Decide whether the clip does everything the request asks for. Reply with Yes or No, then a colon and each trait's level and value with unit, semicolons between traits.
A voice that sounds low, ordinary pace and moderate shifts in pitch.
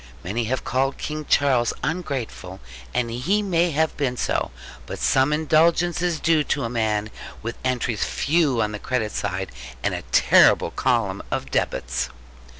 No: low, 130 Hz; average, 155 wpm; wide, 5.8 semitones